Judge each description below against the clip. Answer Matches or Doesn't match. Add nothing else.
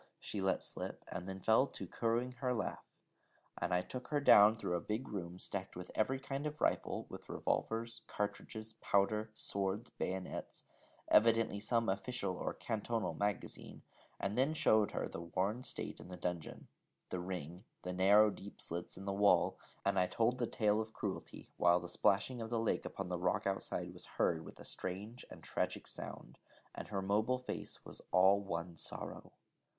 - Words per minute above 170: Matches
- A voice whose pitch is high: Doesn't match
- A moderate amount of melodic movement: Matches